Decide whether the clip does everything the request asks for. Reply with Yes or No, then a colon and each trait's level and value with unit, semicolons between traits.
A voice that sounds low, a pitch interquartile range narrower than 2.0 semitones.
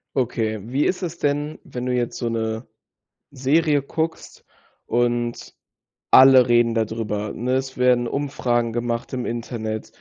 No: low, 120 Hz; narrow, 2.6 semitones